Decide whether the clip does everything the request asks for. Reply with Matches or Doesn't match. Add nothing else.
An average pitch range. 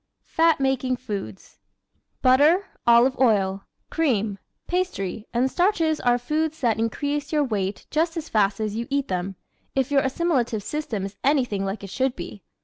Doesn't match